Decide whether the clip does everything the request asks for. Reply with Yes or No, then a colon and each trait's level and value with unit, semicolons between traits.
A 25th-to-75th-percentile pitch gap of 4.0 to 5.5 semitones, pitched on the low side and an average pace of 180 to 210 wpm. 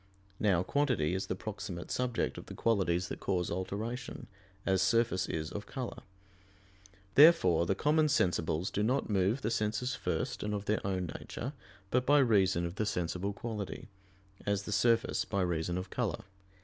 No: average, 4.3 semitones; low, 100 Hz; average, 165 wpm